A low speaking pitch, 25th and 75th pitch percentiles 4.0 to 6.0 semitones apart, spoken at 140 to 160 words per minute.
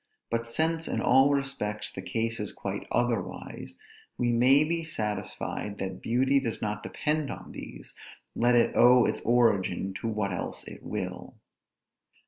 Yes: low, 115 Hz; average, 4.5 semitones; average, 150 wpm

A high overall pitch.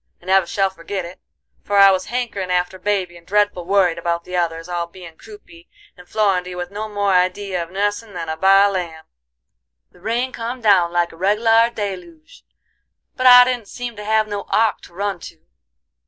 Yes: high, 195 Hz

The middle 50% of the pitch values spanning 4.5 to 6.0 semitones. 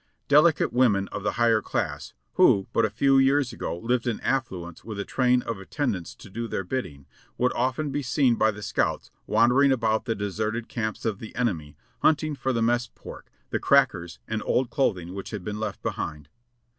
No: average, 4.1 semitones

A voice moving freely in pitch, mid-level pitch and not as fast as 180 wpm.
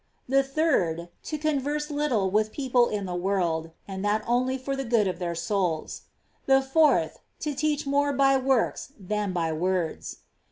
No: wide, 6.7 semitones; high, 240 Hz; average, 165 wpm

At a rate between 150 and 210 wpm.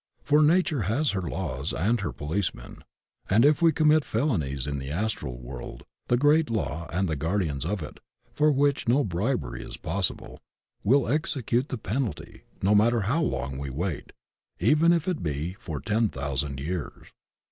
Yes: average, 170 wpm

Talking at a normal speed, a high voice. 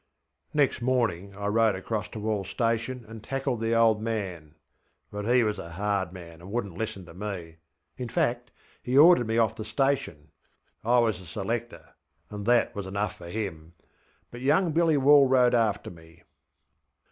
No: average, 170 wpm; low, 110 Hz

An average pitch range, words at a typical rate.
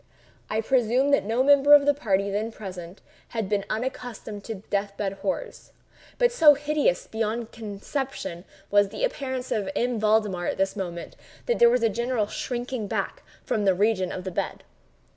Yes: average, 4.6 semitones; average, 175 wpm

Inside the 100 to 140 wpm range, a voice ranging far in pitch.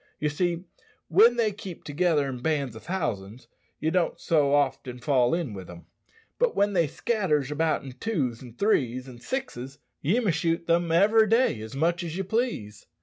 No: average, 185 wpm; wide, 6.7 semitones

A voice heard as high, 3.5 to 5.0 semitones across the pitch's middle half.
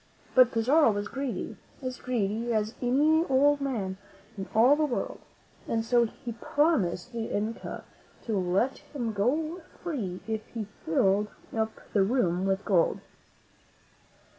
Yes: high, 230 Hz; average, 4.6 semitones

